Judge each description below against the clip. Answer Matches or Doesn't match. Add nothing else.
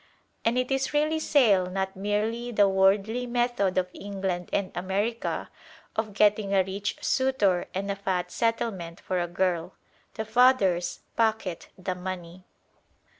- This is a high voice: Matches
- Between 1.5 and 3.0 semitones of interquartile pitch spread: Doesn't match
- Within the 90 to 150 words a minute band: Matches